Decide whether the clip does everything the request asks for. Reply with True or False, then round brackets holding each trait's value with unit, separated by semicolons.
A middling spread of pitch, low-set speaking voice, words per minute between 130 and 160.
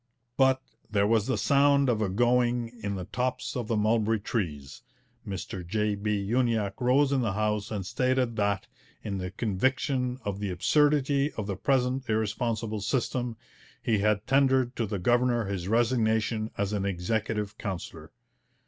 True (3.7 semitones; 110 Hz; 155 wpm)